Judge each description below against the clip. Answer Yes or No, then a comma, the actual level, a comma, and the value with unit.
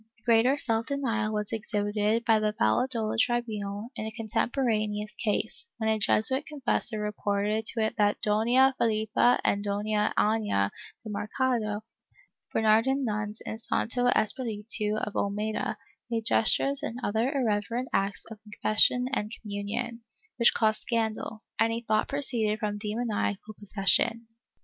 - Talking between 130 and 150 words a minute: Yes, average, 140 wpm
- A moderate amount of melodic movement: No, narrow, 2.1 semitones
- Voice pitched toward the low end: No, high, 220 Hz